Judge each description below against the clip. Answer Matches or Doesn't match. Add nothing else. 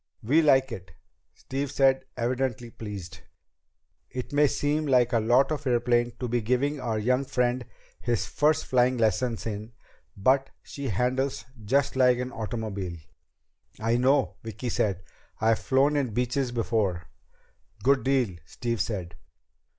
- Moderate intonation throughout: Matches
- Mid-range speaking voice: Doesn't match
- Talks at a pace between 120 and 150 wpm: Matches